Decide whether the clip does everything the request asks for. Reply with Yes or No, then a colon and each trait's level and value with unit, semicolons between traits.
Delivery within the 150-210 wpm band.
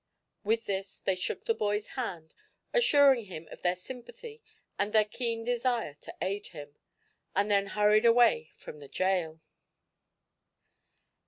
No: average, 140 wpm